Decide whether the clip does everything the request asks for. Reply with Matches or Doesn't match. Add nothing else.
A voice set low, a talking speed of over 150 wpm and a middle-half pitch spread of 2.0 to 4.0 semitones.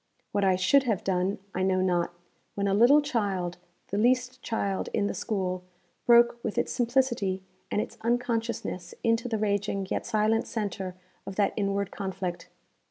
Doesn't match